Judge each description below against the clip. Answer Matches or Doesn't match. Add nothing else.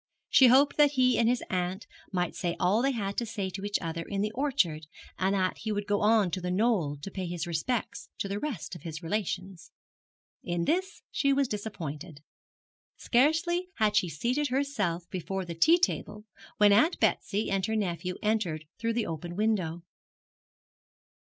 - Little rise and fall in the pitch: Doesn't match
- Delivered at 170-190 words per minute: Matches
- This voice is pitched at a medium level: Doesn't match